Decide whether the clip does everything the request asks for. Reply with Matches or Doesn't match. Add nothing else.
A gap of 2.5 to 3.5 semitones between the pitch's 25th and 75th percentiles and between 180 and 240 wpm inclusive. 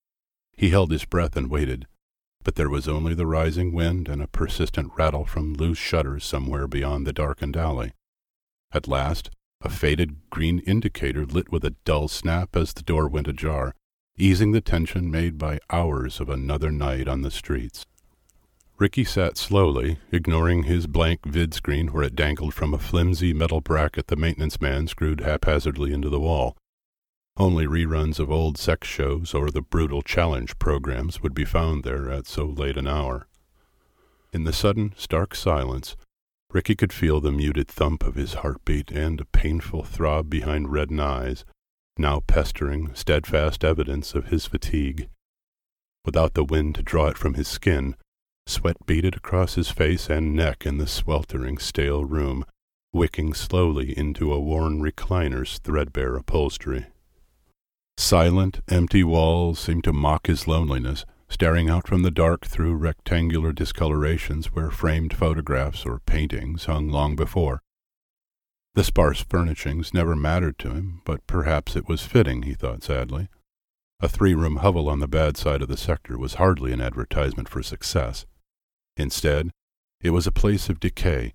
Doesn't match